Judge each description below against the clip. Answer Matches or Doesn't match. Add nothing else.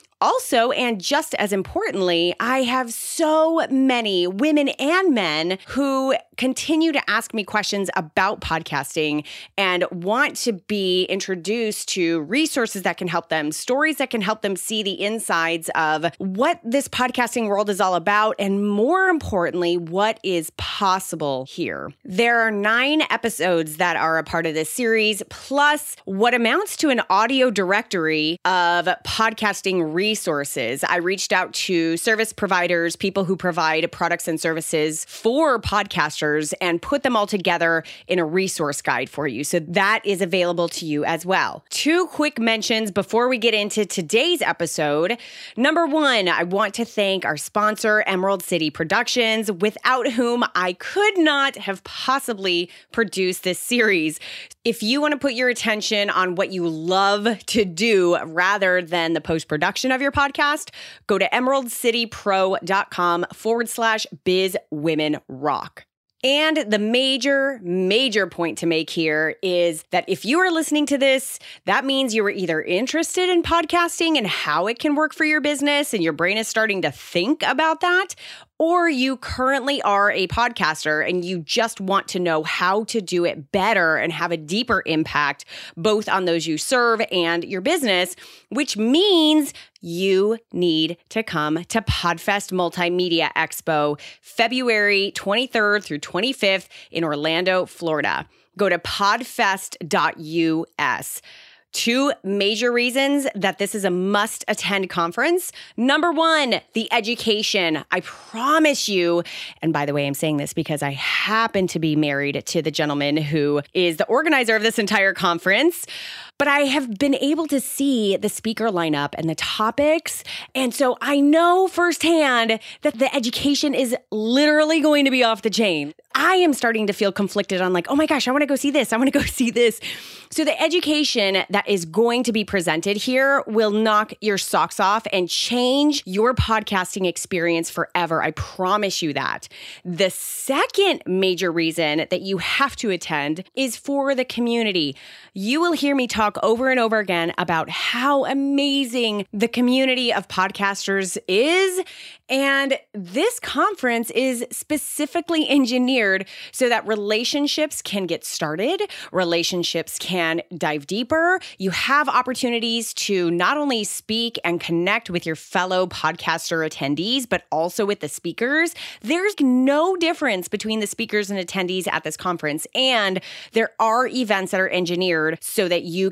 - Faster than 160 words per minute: Doesn't match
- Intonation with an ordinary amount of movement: Doesn't match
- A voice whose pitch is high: Matches